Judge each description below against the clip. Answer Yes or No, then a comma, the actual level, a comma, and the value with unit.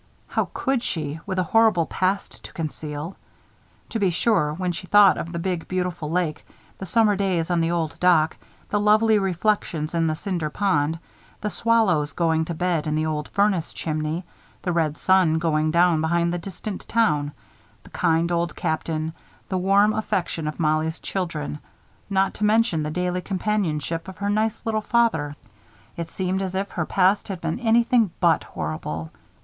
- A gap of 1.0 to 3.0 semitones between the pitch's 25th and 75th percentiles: No, average, 3.9 semitones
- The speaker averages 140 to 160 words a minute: No, average, 175 wpm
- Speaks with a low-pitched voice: No, medium, 175 Hz